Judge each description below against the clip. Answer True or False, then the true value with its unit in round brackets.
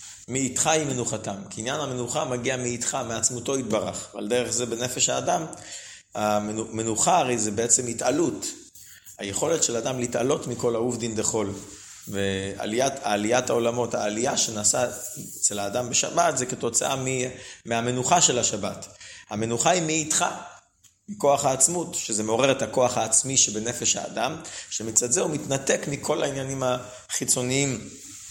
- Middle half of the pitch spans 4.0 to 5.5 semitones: False (3.3 semitones)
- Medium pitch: False (125 Hz)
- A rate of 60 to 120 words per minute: False (130 wpm)